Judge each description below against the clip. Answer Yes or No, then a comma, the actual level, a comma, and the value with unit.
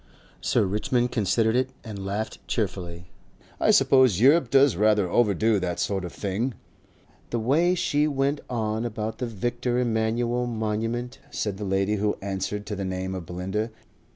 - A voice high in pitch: No, low, 110 Hz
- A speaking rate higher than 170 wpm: No, average, 155 wpm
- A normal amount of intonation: Yes, average, 3.8 semitones